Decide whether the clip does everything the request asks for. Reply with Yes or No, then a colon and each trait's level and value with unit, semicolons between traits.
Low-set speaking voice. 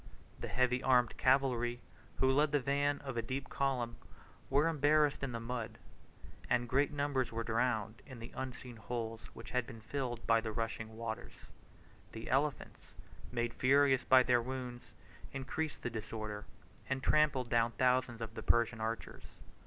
Yes: low, 125 Hz